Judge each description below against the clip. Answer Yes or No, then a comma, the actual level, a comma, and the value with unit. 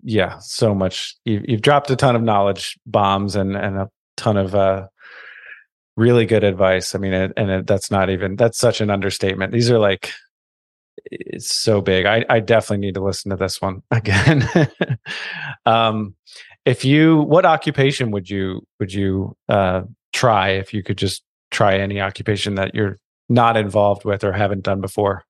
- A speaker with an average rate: Yes, average, 170 wpm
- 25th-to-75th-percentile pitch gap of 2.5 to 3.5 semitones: Yes, average, 2.9 semitones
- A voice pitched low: Yes, low, 100 Hz